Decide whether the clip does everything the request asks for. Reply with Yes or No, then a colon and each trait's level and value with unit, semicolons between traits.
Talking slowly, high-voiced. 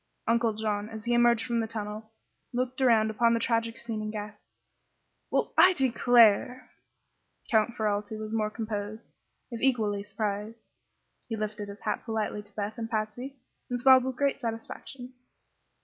No: average, 155 wpm; high, 225 Hz